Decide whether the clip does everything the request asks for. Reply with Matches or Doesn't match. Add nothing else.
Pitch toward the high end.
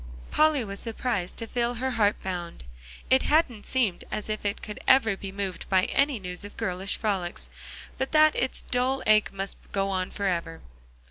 Matches